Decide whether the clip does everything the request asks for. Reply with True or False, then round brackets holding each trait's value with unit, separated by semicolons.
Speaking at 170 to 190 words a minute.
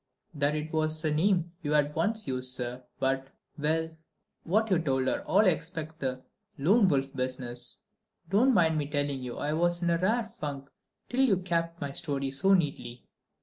True (175 wpm)